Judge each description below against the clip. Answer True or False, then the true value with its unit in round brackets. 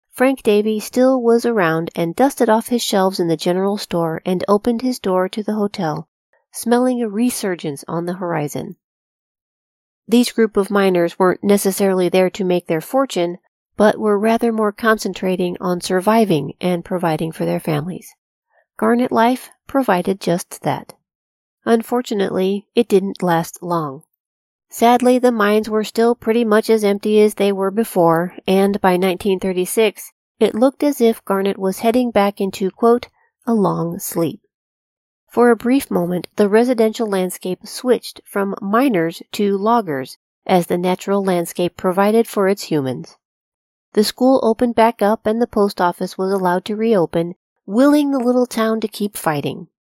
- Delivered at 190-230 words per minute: False (155 wpm)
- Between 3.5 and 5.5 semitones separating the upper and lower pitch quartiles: True (4.2 semitones)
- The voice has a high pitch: True (200 Hz)